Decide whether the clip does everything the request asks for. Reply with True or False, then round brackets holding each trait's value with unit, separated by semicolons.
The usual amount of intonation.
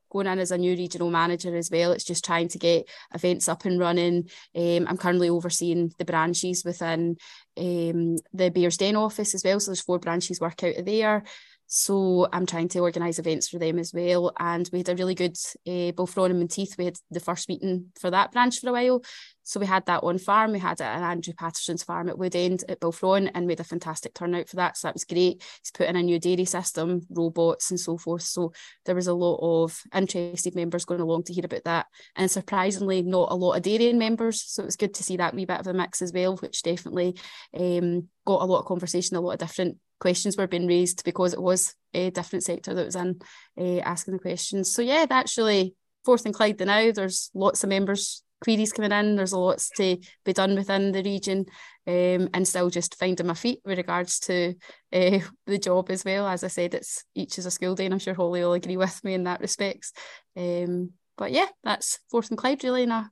False (1.8 semitones)